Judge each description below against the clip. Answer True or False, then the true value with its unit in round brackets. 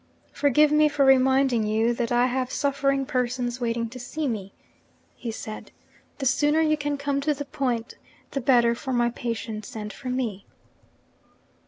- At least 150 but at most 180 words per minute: True (165 wpm)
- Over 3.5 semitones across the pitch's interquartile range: False (3.0 semitones)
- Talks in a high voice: True (255 Hz)